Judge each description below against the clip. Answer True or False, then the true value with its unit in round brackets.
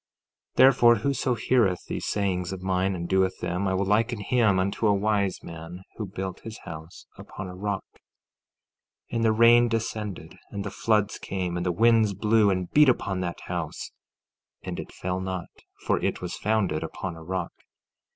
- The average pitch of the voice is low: True (100 Hz)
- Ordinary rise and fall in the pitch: True (3.2 semitones)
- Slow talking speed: False (180 wpm)